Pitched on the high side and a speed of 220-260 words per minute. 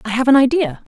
Yes: very high, 250 Hz; fast, 250 wpm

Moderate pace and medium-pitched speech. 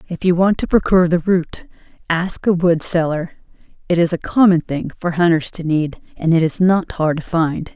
No: fast, 210 wpm; medium, 170 Hz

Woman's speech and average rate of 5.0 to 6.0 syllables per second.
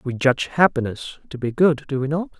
No: male; 5.7 syllables/s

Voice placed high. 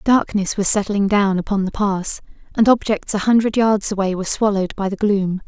Yes: high, 200 Hz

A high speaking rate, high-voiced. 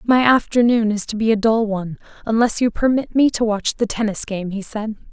Yes: fast, 225 wpm; high, 220 Hz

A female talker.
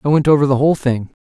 No: male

